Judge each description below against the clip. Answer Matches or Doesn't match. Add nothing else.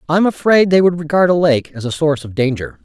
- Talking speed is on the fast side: Matches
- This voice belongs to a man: Matches